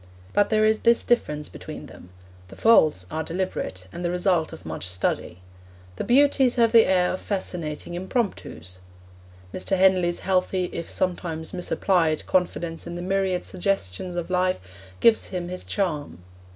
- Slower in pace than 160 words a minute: Yes, average, 150 wpm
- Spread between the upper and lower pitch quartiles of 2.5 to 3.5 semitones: Yes, average, 3.2 semitones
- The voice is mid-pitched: Yes, medium, 180 Hz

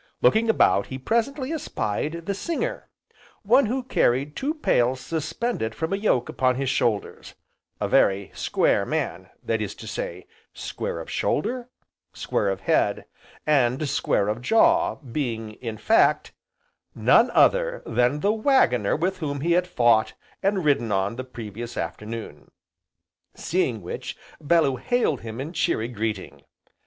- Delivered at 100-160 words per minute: Yes, average, 145 wpm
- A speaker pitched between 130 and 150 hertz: Yes, medium, 140 Hz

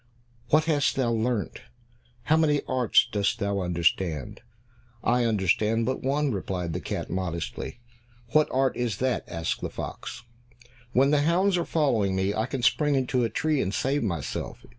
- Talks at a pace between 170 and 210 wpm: No, average, 160 wpm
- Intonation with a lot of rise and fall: Yes, wide, 6.5 semitones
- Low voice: Yes, low, 120 Hz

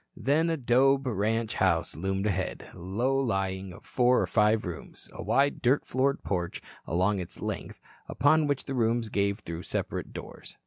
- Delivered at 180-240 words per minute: No, average, 170 wpm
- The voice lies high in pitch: No, low, 110 Hz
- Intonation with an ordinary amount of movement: No, wide, 5.7 semitones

